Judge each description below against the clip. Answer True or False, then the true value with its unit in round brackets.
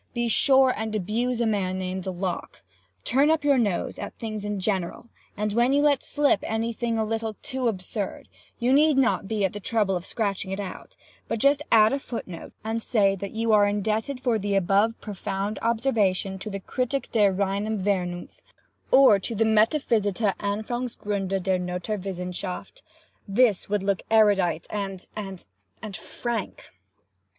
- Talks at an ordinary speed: True (160 wpm)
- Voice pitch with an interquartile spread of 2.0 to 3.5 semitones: True (3.2 semitones)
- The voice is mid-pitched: False (210 Hz)